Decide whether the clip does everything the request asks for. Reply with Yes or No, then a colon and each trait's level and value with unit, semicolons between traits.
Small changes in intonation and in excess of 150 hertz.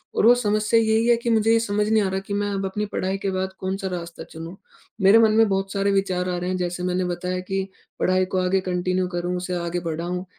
Yes: narrow, 2.3 semitones; high, 190 Hz